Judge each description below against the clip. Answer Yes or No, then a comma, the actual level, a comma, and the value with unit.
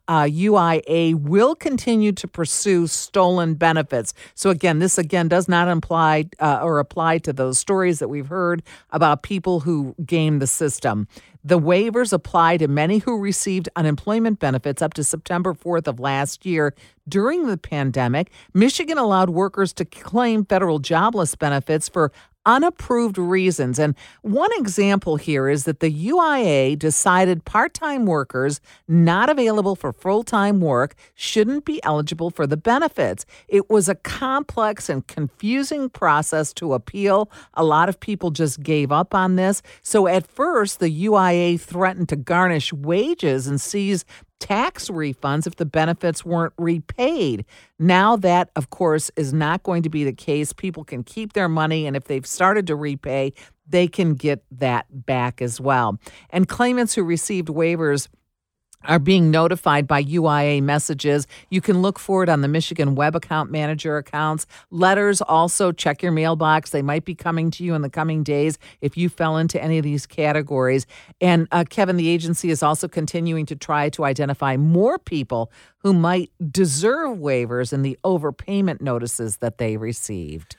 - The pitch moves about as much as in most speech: Yes, average, 4.2 semitones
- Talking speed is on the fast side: No, average, 165 wpm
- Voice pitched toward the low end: No, medium, 165 Hz